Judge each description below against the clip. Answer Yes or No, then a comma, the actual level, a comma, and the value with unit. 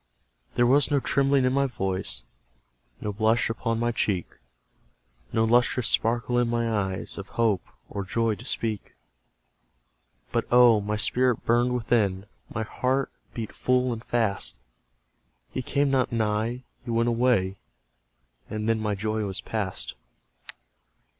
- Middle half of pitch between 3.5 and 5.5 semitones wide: No, average, 2.7 semitones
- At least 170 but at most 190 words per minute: No, average, 140 wpm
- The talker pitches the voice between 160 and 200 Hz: No, low, 115 Hz